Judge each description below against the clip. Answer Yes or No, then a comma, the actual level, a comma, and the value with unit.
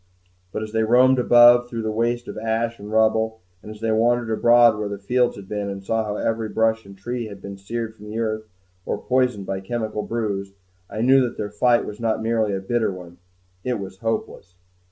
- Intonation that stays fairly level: Yes, narrow, 2.3 semitones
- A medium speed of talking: No, fast, 215 wpm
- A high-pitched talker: No, low, 110 Hz